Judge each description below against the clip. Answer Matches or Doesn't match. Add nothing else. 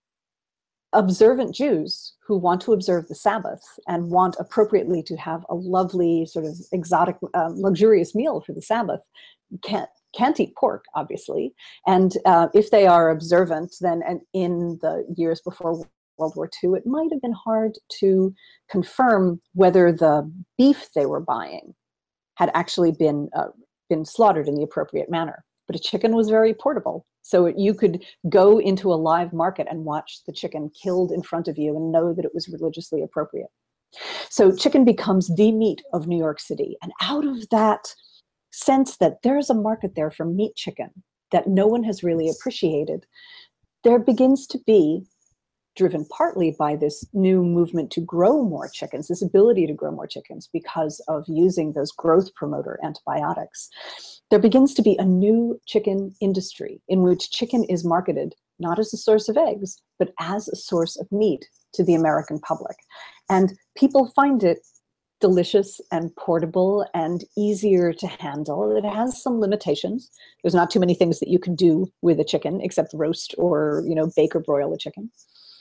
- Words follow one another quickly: Doesn't match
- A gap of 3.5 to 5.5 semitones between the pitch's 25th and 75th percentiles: Matches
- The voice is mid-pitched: Matches